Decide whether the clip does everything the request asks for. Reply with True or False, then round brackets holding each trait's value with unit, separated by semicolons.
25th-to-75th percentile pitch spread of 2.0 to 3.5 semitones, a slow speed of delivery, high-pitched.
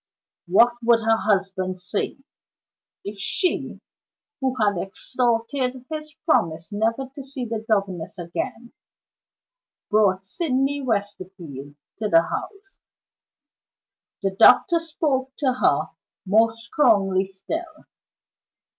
False (5.4 semitones; 105 wpm; 225 Hz)